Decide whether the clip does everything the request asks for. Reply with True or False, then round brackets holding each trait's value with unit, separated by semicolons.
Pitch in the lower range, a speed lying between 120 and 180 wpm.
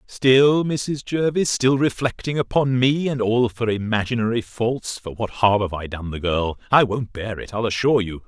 False (115 Hz; 190 wpm)